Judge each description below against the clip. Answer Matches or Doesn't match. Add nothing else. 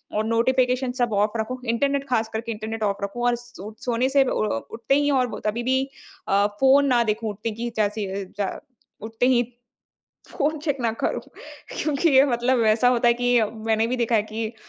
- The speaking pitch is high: Matches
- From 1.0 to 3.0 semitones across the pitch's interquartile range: Matches